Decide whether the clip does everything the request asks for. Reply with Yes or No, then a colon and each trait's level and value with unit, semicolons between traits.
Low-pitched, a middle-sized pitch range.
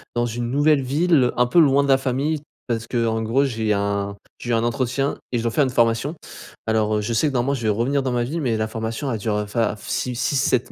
Yes: low, 120 Hz; average, 3.4 semitones